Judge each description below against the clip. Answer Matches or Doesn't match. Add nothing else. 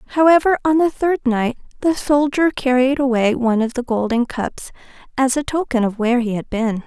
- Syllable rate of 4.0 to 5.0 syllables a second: Doesn't match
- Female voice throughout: Matches